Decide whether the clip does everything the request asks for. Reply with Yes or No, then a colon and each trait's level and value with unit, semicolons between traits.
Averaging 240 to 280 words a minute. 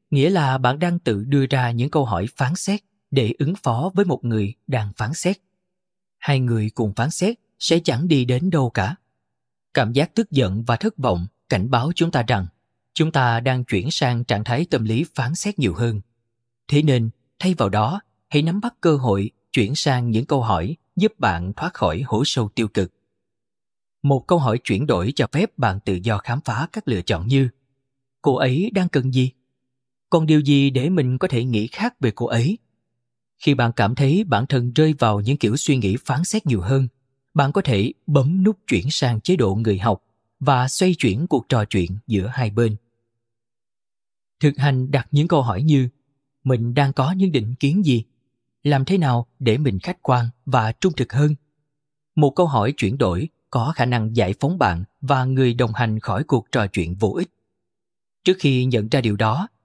No: average, 200 wpm